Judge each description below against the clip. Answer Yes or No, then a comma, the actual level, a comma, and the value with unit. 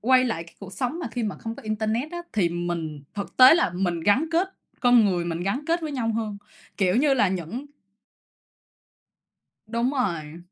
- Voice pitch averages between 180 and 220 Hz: Yes, high, 215 Hz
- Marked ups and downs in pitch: Yes, wide, 6.4 semitones